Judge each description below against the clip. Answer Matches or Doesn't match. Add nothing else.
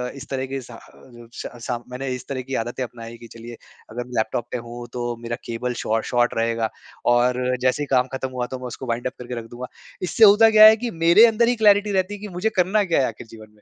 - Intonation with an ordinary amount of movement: Doesn't match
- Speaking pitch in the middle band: Doesn't match